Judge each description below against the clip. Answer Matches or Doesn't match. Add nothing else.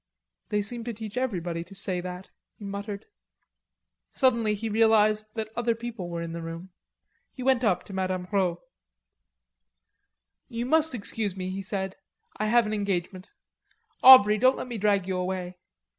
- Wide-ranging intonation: Doesn't match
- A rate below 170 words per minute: Matches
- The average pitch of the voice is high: Matches